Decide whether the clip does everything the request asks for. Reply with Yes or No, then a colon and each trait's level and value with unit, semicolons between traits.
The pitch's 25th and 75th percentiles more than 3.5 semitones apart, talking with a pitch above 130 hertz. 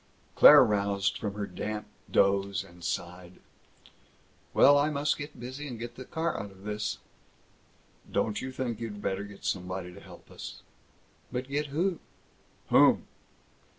No: average, 5.1 semitones; low, 105 Hz